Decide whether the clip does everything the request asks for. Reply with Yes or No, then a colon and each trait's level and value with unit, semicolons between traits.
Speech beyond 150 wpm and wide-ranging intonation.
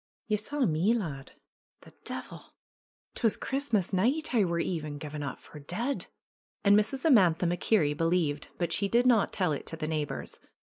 Yes: average, 170 wpm; wide, 6.4 semitones